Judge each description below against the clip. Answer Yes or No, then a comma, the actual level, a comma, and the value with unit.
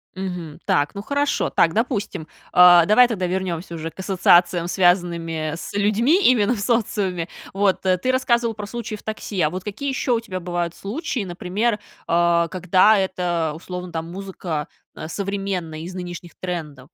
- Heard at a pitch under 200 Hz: Yes, medium, 185 Hz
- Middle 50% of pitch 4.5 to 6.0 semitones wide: No, average, 3.3 semitones